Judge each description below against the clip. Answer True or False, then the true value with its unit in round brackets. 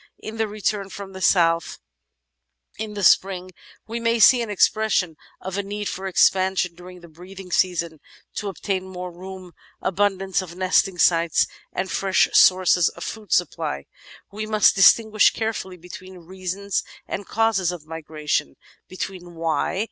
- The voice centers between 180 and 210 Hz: True (190 Hz)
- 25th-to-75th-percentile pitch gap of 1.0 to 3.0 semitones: True (2.4 semitones)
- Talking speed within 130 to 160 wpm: True (155 wpm)